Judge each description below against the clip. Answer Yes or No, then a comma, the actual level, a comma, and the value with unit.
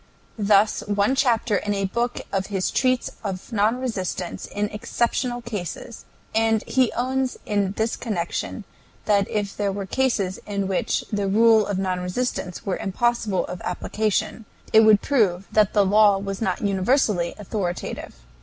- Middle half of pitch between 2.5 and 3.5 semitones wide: Yes, average, 2.9 semitones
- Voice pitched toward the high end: Yes, high, 205 Hz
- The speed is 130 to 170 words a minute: Yes, average, 155 wpm